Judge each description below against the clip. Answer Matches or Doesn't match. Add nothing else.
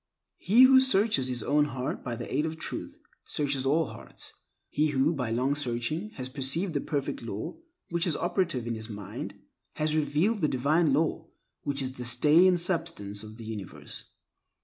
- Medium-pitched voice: Matches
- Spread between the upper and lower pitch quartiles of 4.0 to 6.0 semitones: Matches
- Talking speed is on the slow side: Doesn't match